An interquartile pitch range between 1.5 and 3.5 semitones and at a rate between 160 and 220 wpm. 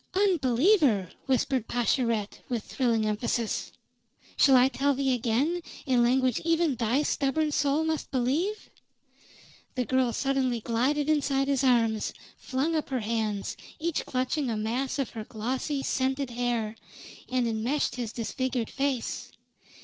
No: average, 3.2 semitones; slow, 135 wpm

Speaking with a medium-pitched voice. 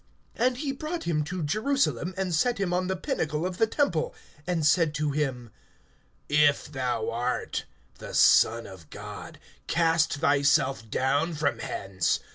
Yes: medium, 155 Hz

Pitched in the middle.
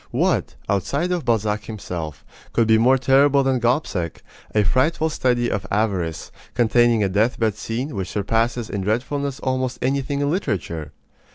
No: low, 115 Hz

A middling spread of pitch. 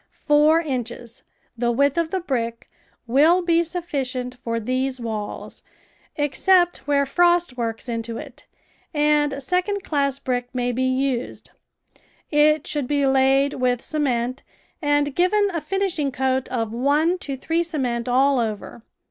Yes: average, 4.0 semitones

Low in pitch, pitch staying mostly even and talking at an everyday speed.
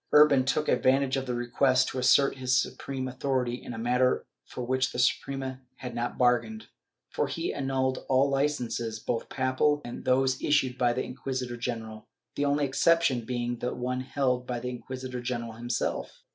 Yes: low, 130 Hz; narrow, 1.7 semitones; average, 175 wpm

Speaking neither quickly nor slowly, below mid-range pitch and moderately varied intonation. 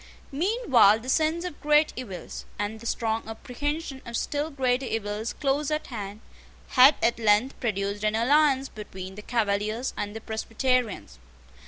No: average, 150 wpm; high, 235 Hz; average, 4.7 semitones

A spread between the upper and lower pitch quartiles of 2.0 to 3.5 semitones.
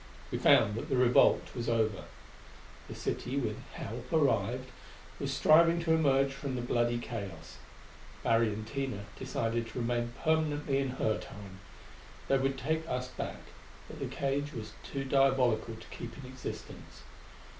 Yes: average, 3.2 semitones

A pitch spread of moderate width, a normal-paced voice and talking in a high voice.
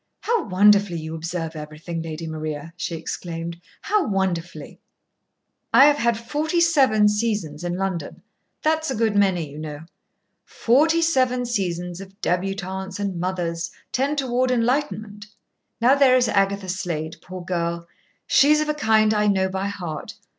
No: wide, 6.3 semitones; average, 145 wpm; high, 195 Hz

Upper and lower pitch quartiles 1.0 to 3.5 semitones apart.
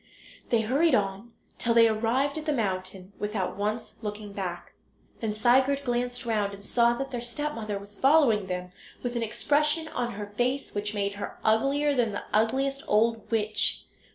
No: average, 3.9 semitones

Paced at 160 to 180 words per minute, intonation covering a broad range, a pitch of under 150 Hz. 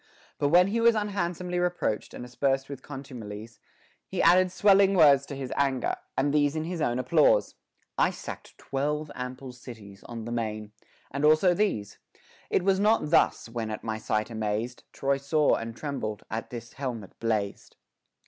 Yes: average, 165 wpm; wide, 6.3 semitones; low, 135 Hz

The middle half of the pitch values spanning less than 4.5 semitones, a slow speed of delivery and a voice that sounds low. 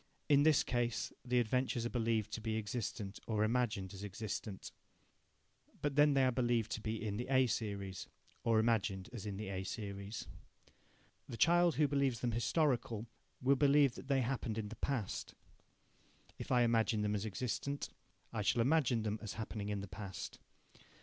No: average, 3.5 semitones; average, 175 wpm; low, 115 Hz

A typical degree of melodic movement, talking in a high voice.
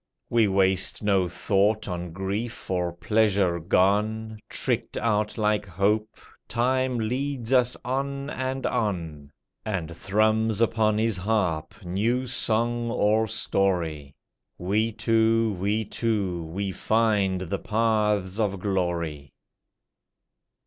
No: average, 3.3 semitones; low, 105 Hz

